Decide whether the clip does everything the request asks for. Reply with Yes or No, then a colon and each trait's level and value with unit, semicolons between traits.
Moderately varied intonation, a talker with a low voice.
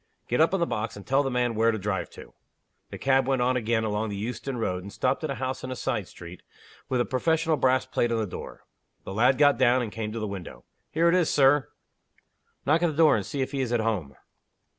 Yes: average, 3.9 semitones; low, 125 Hz